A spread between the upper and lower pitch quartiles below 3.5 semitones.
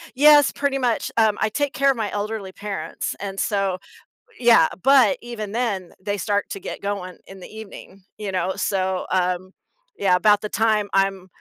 Yes: average, 2.9 semitones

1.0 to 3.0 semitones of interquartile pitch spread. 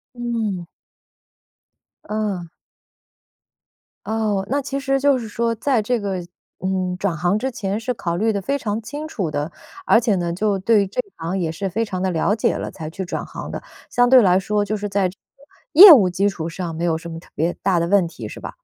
No: average, 4.2 semitones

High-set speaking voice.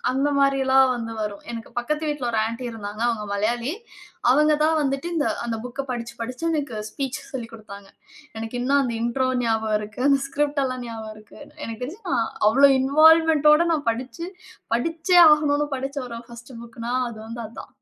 Yes: very high, 255 Hz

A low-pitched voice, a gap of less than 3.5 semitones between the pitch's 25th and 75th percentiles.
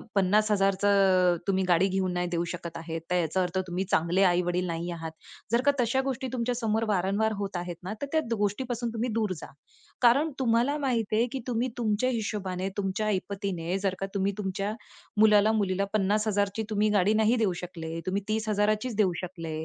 No: high, 200 Hz; average, 3.1 semitones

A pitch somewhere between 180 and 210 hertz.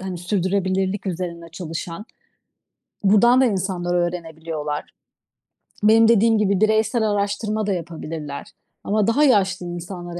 Yes: high, 190 Hz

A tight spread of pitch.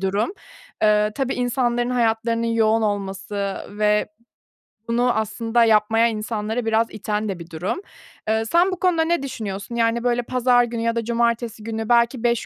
Yes: narrow, 2.1 semitones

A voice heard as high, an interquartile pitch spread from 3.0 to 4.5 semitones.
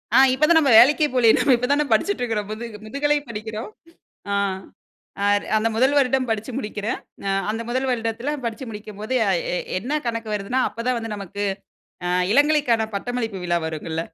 Yes: high, 230 Hz; average, 3.5 semitones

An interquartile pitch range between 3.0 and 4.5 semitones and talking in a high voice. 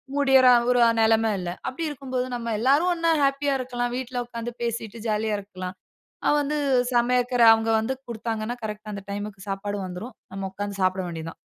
Yes: average, 3.7 semitones; high, 230 Hz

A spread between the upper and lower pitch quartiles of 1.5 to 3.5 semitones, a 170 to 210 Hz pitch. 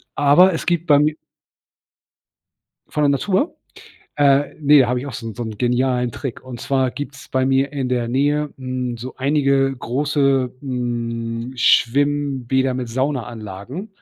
No: average, 2.7 semitones; low, 130 Hz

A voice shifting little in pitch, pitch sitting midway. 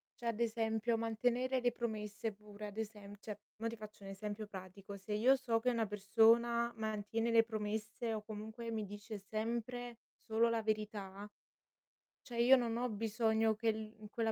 No: narrow, 1.7 semitones; high, 220 Hz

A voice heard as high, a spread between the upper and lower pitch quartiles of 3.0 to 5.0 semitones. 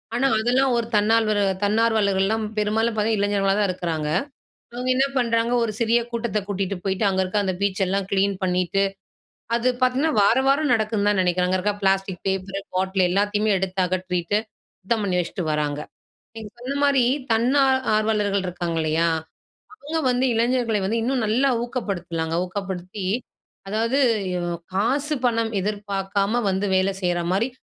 Yes: high, 205 Hz; average, 3.5 semitones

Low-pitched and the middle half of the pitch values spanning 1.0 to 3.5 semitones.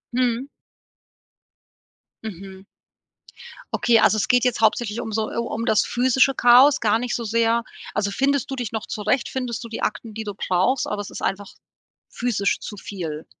No: high, 225 Hz; average, 3.1 semitones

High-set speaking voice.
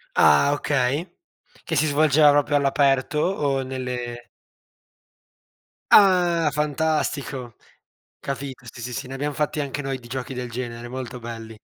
No: low, 135 Hz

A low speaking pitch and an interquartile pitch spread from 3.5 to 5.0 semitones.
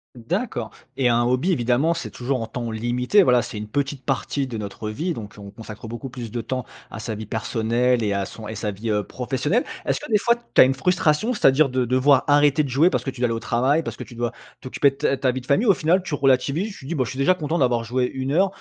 Yes: low, 130 Hz; average, 3.9 semitones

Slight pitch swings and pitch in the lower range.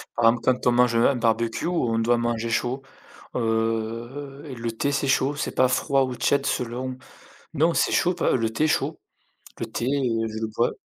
No: average, 3.1 semitones; low, 120 Hz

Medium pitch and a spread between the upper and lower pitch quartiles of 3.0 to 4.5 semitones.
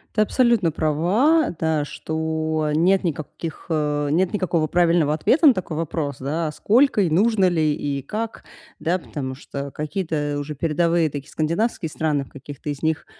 Yes: medium, 160 Hz; average, 3.6 semitones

